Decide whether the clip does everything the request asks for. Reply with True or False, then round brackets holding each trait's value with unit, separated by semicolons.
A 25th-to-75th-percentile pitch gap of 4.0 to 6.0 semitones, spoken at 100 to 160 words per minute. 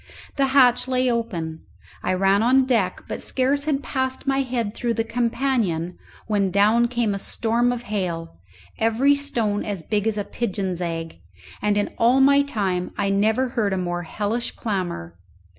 False (4.5 semitones; 170 wpm)